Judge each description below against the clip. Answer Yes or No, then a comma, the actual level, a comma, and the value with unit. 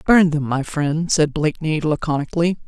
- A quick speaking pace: No, average, 155 wpm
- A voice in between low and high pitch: Yes, medium, 155 Hz